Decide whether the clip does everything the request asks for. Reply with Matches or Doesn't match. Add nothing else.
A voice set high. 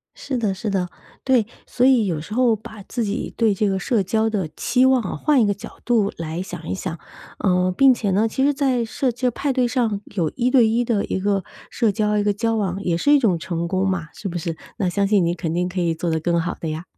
Matches